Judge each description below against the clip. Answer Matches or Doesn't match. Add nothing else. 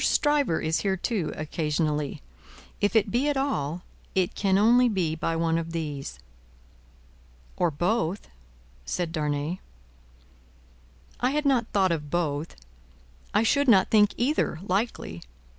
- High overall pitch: Doesn't match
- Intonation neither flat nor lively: Doesn't match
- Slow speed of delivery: Matches